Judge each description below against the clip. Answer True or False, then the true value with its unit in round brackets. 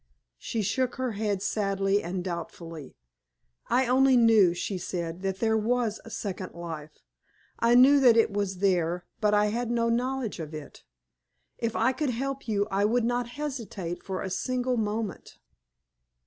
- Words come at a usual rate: True (160 wpm)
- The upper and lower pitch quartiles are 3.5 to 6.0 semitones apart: True (4.4 semitones)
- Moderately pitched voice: False (210 Hz)